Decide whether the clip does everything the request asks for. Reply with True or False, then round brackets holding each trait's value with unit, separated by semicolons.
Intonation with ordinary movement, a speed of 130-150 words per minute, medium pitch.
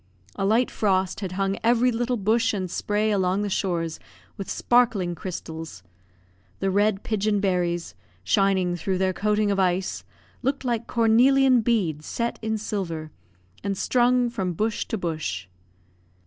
False (3.8 semitones; 145 wpm; 200 Hz)